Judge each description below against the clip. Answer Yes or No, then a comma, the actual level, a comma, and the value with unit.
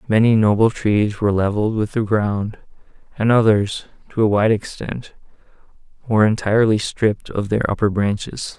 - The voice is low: Yes, low, 105 Hz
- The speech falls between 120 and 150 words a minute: Yes, average, 145 wpm